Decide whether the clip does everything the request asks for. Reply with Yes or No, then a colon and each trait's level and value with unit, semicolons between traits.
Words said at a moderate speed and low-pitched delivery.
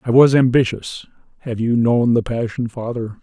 Yes: average, 150 wpm; low, 120 Hz